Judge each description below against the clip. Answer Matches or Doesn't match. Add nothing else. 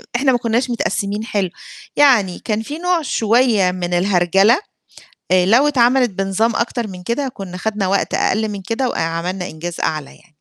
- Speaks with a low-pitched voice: Doesn't match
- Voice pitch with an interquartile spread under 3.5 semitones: Doesn't match